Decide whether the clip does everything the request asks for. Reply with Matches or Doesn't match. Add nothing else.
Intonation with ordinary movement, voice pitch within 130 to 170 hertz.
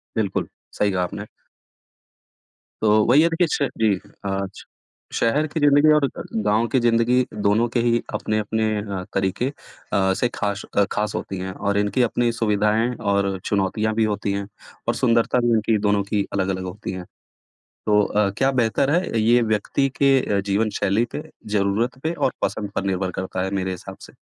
Doesn't match